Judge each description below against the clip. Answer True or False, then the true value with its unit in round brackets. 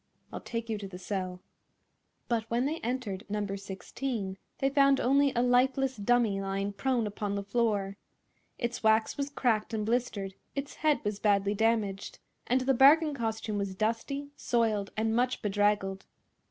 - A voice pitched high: True (220 Hz)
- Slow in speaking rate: False (160 wpm)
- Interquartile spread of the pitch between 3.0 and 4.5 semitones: True (4.0 semitones)